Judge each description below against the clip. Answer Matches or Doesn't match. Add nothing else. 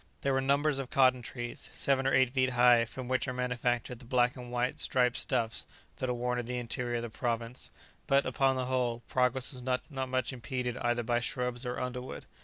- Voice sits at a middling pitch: Doesn't match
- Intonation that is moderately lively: Doesn't match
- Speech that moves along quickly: Matches